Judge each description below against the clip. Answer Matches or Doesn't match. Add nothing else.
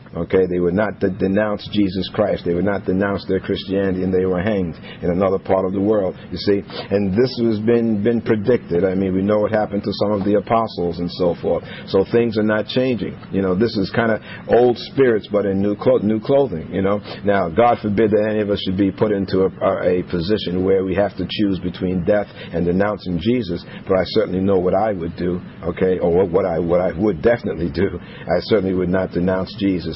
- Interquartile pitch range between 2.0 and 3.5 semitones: Matches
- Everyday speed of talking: Doesn't match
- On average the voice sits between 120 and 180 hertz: Doesn't match